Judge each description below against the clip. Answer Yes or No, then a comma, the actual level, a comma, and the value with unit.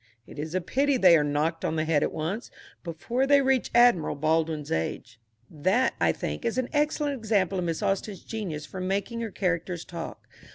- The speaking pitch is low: No, medium, 185 Hz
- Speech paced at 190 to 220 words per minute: Yes, average, 200 wpm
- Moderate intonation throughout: No, wide, 6.7 semitones